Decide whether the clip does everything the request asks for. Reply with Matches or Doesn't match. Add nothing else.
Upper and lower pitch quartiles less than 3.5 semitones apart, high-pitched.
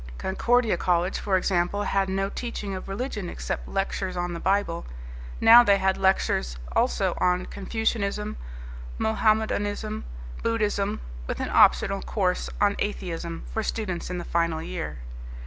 Matches